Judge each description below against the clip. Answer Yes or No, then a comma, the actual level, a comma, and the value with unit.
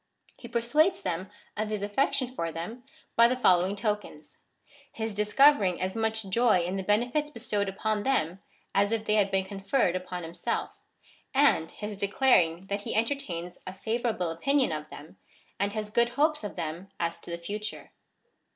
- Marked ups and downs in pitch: No, average, 4.4 semitones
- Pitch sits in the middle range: No, high, 205 Hz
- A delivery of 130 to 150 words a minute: No, average, 180 wpm